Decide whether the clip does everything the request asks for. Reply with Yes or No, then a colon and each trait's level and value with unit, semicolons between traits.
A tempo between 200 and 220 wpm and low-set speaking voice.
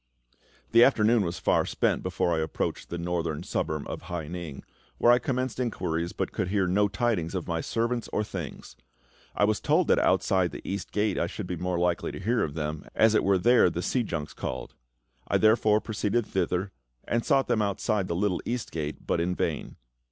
Yes: fast, 205 wpm; very low, 95 Hz